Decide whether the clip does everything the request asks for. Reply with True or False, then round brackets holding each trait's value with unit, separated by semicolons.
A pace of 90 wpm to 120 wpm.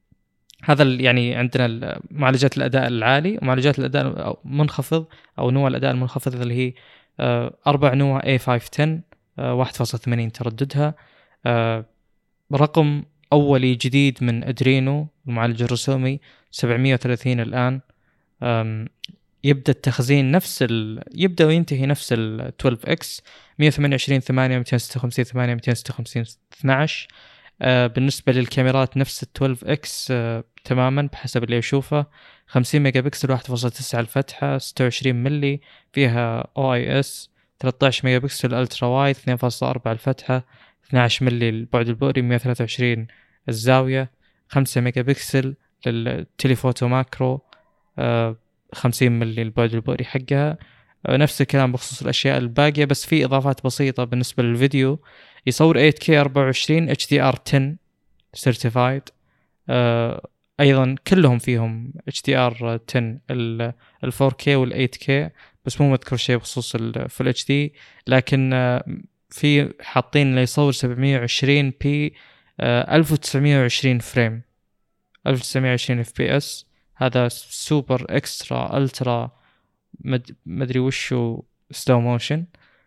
True (100 wpm)